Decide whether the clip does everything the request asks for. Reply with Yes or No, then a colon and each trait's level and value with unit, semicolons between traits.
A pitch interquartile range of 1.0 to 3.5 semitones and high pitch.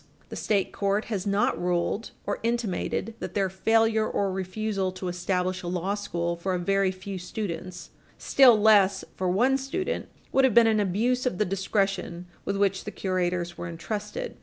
Yes: average, 3.1 semitones; high, 195 Hz